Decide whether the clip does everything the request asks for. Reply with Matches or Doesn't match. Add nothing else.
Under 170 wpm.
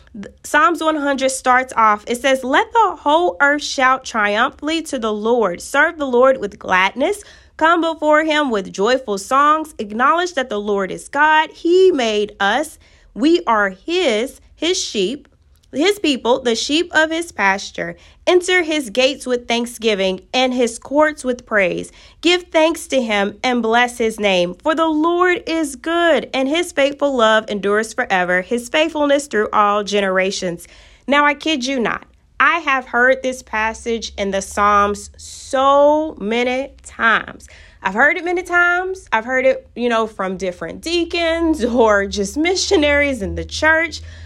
Matches